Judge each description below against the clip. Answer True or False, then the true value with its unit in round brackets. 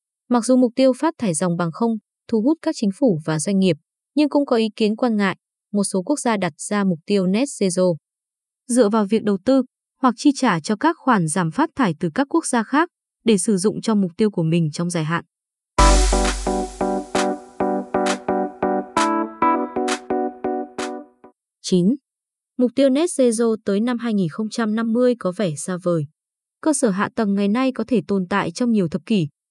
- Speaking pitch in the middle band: False (215 Hz)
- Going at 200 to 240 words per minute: False (185 wpm)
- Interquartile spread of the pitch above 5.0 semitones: True (5.6 semitones)